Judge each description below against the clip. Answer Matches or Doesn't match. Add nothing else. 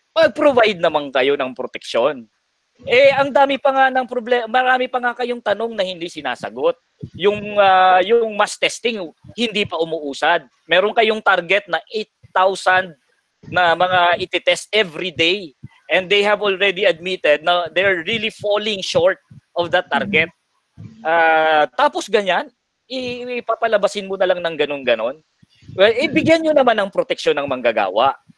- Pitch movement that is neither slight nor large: Doesn't match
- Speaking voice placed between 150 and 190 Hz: Doesn't match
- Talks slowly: Doesn't match